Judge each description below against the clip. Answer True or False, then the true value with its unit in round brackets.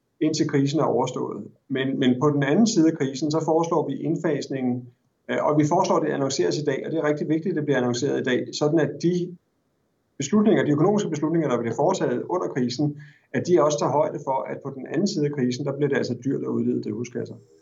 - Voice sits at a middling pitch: True (150 Hz)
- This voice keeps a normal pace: False (235 wpm)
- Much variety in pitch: False (3.7 semitones)